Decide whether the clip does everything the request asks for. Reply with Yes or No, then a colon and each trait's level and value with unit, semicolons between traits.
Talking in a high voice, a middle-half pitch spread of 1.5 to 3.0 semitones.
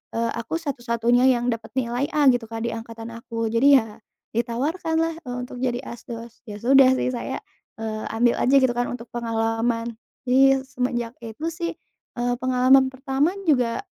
Yes: high, 245 Hz; narrow, 2.4 semitones